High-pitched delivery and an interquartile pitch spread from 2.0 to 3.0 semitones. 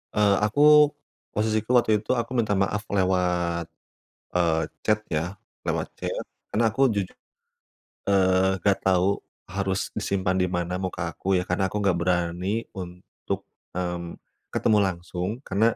No: very low, 95 Hz; narrow, 2.5 semitones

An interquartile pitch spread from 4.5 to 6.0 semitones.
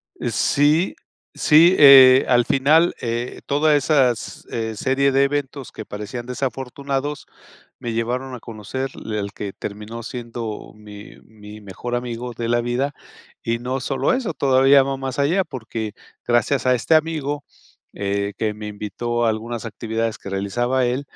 No: average, 3.6 semitones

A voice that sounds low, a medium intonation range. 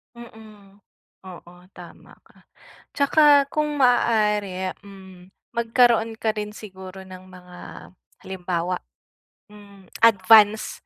No: high, 205 Hz; average, 3.3 semitones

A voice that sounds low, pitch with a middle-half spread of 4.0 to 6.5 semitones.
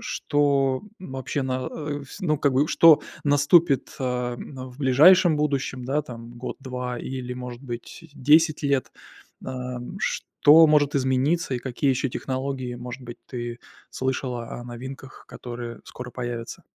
No: low, 130 Hz; narrow, 2.6 semitones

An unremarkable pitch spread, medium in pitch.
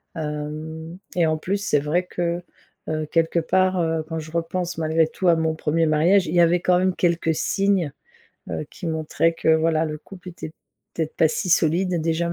No: narrow, 2.0 semitones; medium, 165 Hz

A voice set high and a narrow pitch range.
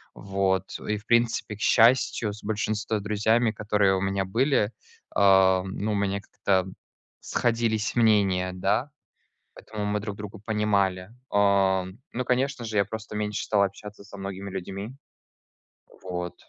No: low, 105 Hz; narrow, 2.1 semitones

